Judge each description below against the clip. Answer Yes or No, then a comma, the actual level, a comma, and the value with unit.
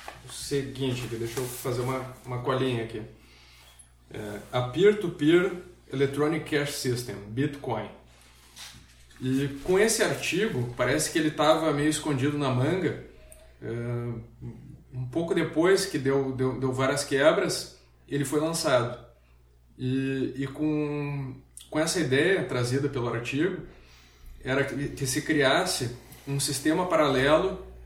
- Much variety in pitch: No, average, 3.9 semitones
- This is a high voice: No, low, 130 Hz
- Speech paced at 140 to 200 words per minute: No, average, 125 wpm